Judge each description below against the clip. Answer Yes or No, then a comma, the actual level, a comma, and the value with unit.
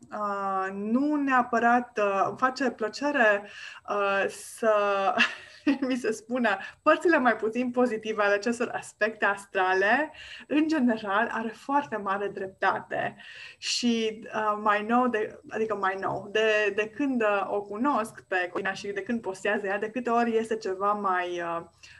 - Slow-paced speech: No, average, 145 wpm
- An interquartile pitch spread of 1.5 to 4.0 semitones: Yes, average, 3.2 semitones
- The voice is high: Yes, high, 215 Hz